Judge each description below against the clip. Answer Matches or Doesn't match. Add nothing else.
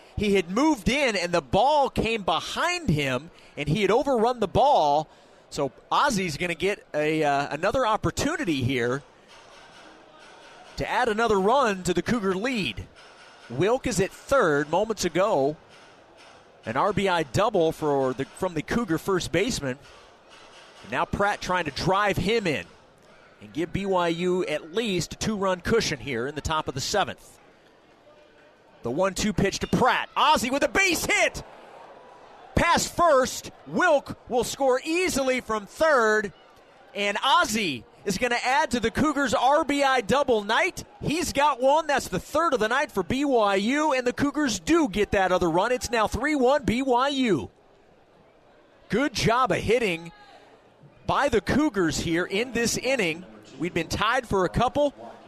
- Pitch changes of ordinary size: Doesn't match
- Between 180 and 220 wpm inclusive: Doesn't match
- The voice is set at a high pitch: Matches